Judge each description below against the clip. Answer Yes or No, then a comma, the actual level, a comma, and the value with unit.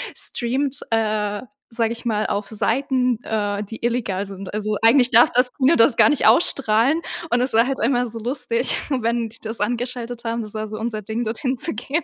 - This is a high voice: Yes, high, 230 Hz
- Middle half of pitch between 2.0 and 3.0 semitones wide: Yes, narrow, 2.5 semitones